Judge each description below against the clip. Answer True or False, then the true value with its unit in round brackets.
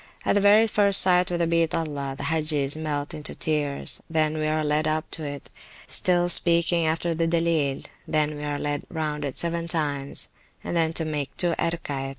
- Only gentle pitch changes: True (2.3 semitones)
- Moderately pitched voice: True (155 Hz)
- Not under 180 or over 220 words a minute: True (190 wpm)